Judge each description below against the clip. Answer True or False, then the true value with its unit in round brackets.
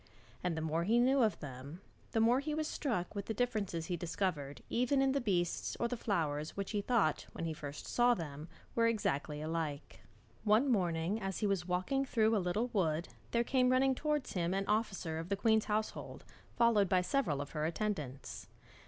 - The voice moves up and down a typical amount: False (6.3 semitones)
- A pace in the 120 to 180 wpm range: False (195 wpm)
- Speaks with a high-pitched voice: True (200 Hz)